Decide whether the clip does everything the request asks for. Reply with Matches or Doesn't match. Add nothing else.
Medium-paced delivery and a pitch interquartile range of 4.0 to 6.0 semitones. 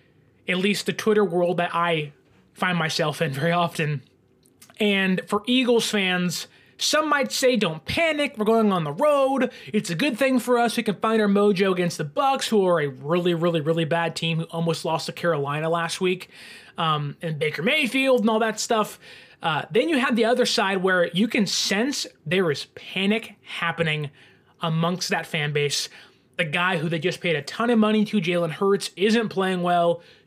Matches